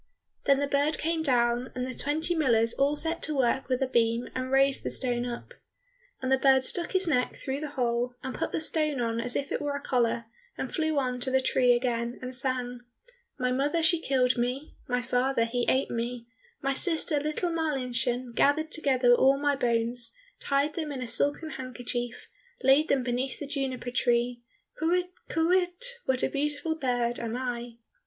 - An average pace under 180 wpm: No, average, 190 wpm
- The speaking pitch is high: Yes, very high, 260 Hz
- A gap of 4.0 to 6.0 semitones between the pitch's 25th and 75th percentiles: No, average, 3.2 semitones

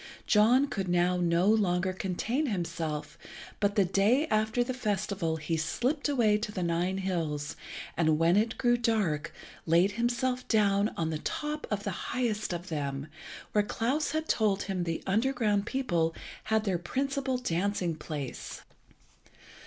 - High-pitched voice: Yes, high, 200 Hz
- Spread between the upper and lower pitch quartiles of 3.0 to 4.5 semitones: No, wide, 5.6 semitones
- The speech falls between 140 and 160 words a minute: Yes, average, 150 wpm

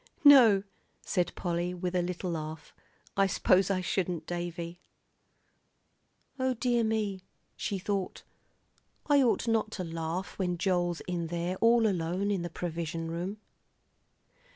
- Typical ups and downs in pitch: Yes, average, 3.0 semitones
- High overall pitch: No, medium, 180 Hz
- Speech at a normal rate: No, slow, 130 wpm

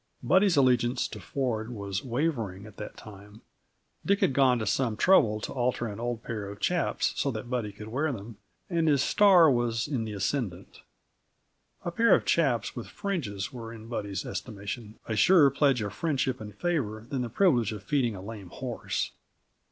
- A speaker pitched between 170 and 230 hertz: No, low, 120 Hz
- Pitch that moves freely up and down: No, average, 4.7 semitones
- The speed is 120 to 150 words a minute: No, average, 185 wpm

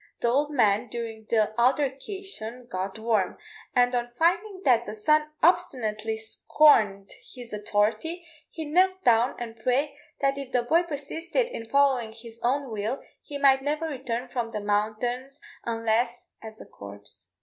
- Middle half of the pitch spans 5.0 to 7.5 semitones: No, average, 4.5 semitones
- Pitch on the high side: Yes, high, 245 Hz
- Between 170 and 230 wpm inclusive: No, average, 150 wpm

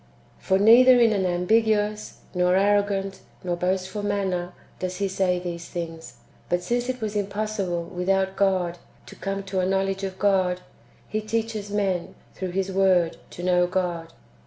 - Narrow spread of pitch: Yes, narrow, 2.2 semitones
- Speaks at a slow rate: No, average, 160 wpm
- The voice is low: No, high, 190 Hz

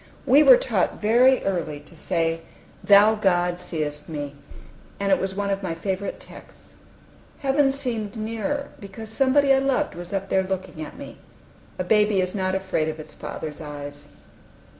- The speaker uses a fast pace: No, average, 165 wpm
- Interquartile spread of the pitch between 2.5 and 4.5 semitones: No, average, 4.9 semitones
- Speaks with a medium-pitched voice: No, high, 195 Hz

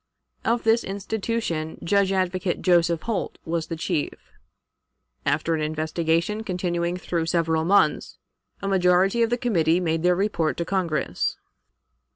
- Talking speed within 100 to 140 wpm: Yes, slow, 135 wpm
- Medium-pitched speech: Yes, medium, 175 Hz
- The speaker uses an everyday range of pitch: Yes, average, 3.3 semitones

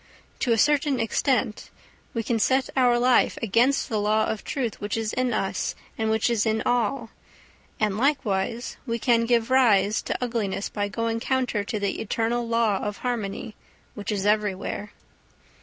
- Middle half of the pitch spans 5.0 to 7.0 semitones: No, average, 2.8 semitones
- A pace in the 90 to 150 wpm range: No, average, 165 wpm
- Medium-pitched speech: No, high, 225 Hz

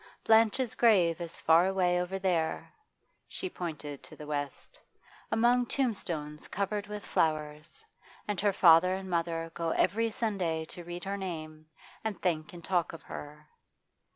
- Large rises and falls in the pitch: No, average, 4.0 semitones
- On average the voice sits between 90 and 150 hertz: No, medium, 175 Hz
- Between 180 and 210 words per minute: No, average, 150 wpm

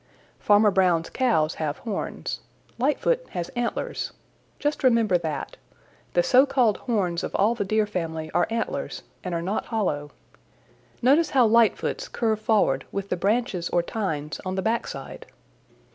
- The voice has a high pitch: Yes, high, 205 Hz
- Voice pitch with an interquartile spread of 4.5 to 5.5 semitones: Yes, average, 5.1 semitones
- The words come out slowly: No, average, 150 wpm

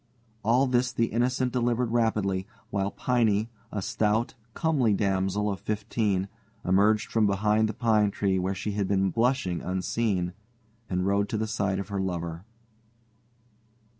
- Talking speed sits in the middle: Yes, average, 145 wpm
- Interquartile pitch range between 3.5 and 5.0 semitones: No, average, 3.1 semitones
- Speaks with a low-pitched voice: Yes, low, 105 Hz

